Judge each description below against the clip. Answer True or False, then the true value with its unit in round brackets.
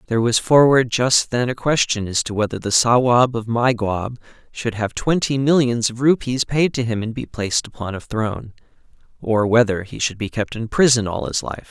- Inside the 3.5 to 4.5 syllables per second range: False (5.1 syllables/s)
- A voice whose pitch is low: True (120 Hz)